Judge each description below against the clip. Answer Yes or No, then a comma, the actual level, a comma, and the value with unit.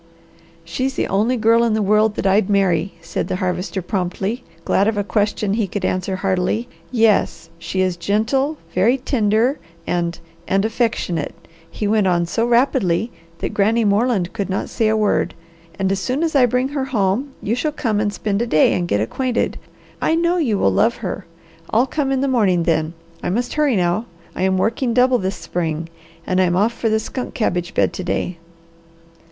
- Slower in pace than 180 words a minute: No, average, 190 wpm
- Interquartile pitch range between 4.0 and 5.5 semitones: Yes, average, 4.4 semitones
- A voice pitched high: Yes, high, 210 Hz